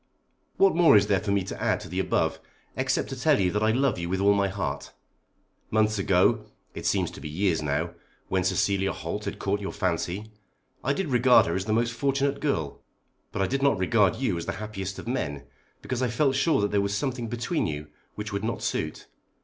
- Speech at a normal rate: No, fast, 225 wpm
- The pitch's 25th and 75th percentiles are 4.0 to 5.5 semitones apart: Yes, average, 4.4 semitones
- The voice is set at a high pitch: No, low, 105 Hz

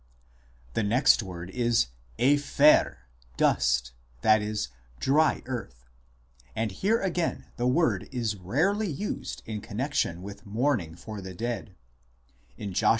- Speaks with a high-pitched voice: No, low, 110 Hz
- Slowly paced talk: Yes, slow, 130 wpm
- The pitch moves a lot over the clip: Yes, wide, 6.7 semitones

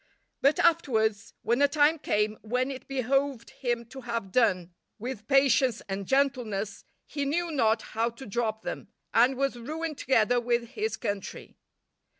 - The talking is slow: No, average, 155 wpm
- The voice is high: Yes, high, 245 Hz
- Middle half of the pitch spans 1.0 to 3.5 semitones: No, average, 3.9 semitones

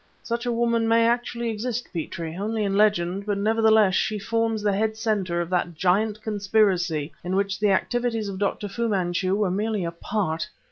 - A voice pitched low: No, high, 205 Hz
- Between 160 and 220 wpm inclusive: Yes, average, 185 wpm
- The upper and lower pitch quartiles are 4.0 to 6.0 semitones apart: No, average, 3.0 semitones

